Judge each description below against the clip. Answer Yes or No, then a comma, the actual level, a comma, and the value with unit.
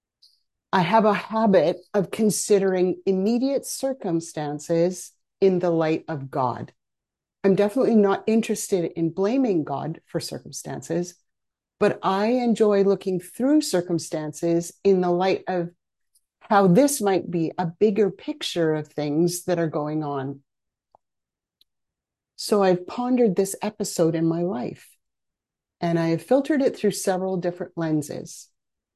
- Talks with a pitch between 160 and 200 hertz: Yes, medium, 185 Hz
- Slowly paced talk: Yes, slow, 130 wpm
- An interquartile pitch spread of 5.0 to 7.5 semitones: No, average, 3.8 semitones